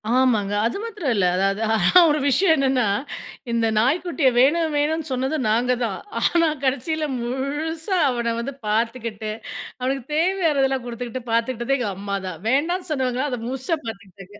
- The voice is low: No, very high, 255 Hz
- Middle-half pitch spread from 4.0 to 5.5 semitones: Yes, average, 4.7 semitones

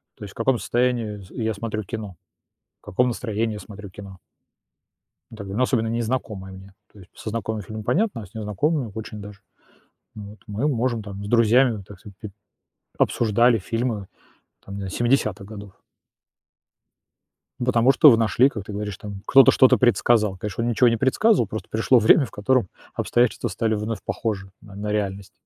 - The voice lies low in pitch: Yes, low, 110 Hz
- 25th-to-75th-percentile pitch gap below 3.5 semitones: Yes, average, 2.8 semitones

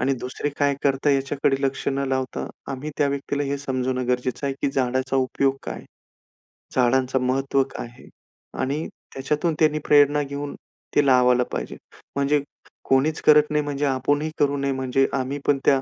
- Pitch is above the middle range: No, low, 135 Hz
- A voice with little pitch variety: Yes, narrow, 1.7 semitones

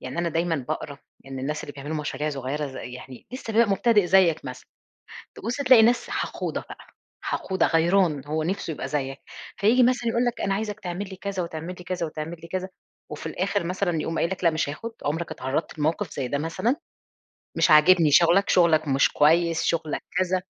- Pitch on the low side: No, medium, 170 Hz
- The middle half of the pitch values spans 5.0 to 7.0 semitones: No, average, 4.3 semitones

